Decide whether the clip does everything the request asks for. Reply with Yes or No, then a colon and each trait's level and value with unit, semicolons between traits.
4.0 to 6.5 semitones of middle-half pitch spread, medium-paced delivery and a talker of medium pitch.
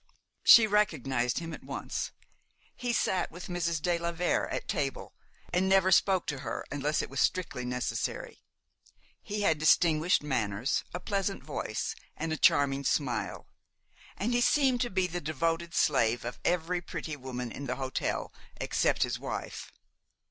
Yes: average, 5.0 semitones; average, 155 wpm; medium, 165 Hz